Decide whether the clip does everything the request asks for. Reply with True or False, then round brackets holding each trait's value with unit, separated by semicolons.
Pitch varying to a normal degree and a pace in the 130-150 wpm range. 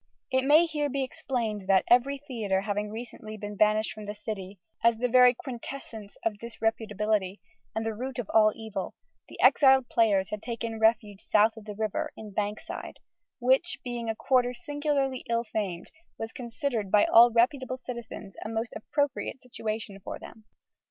False (3.1 semitones; 165 wpm)